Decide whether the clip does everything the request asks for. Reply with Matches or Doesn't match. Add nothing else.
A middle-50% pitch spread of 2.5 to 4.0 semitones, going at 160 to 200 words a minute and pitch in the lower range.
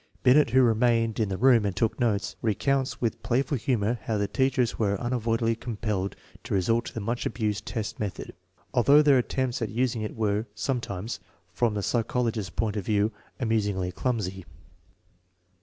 Matches